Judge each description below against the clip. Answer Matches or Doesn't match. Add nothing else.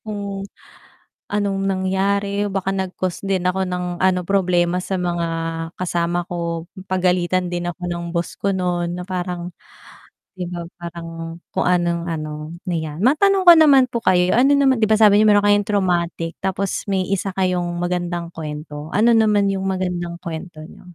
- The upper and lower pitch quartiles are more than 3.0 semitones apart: Doesn't match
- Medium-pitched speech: Matches